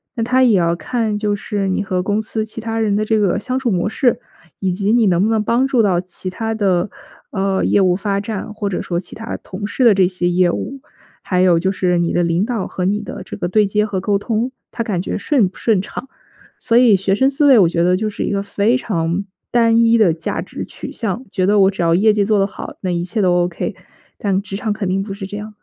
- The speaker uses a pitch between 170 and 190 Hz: No, high, 200 Hz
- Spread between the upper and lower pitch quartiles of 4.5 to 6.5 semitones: No, average, 3.2 semitones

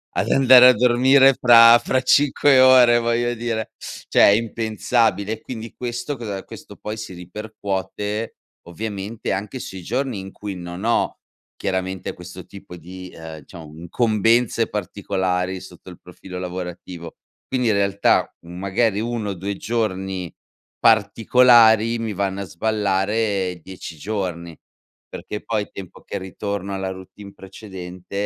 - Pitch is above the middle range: No, low, 100 Hz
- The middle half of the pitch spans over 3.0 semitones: Yes, average, 3.8 semitones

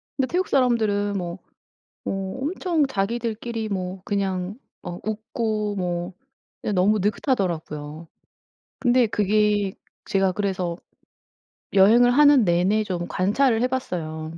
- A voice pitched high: Yes, high, 205 Hz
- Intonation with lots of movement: No, average, 4.3 semitones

